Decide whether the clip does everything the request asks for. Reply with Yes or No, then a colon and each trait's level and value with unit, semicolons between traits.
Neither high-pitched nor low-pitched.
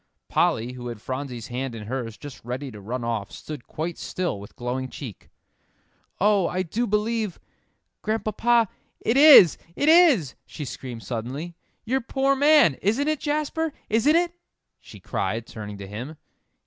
Yes: medium, 155 Hz